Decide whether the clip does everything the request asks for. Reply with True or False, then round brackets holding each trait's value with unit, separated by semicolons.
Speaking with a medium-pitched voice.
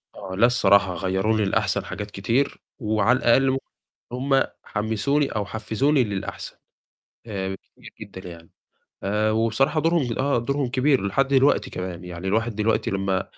False (110 Hz)